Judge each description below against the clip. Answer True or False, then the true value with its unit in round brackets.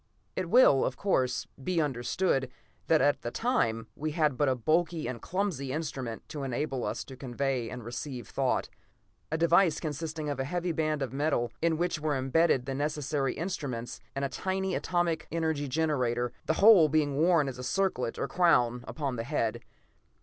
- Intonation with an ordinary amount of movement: True (4.3 semitones)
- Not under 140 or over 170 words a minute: False (180 wpm)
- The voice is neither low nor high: True (145 Hz)